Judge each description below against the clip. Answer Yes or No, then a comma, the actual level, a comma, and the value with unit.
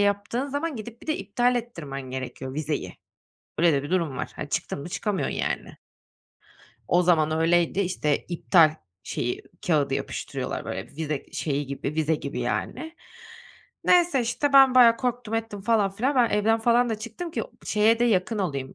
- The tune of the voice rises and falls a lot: Yes, wide, 7.5 semitones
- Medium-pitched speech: No, high, 200 Hz